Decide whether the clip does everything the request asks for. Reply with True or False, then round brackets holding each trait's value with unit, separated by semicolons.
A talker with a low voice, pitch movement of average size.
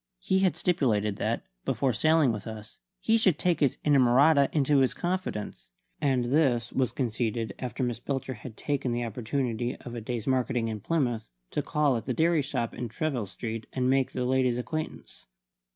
True (125 Hz; 3.7 semitones)